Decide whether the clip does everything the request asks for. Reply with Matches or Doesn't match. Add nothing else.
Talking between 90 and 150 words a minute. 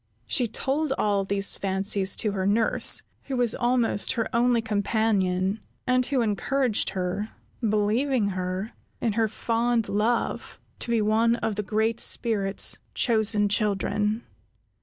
Matches